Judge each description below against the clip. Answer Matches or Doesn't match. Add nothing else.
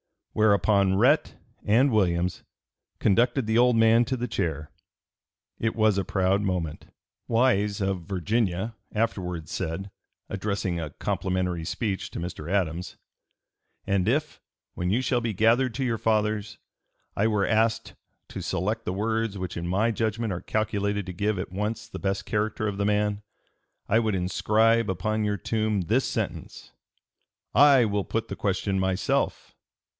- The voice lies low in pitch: Matches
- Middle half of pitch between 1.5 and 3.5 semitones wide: Matches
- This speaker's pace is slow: Doesn't match